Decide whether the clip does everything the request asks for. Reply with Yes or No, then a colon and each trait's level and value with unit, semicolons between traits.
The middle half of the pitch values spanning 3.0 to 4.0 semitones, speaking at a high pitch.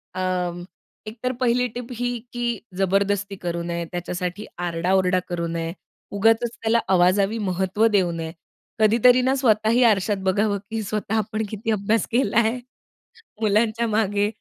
Yes: average, 3.5 semitones; high, 205 Hz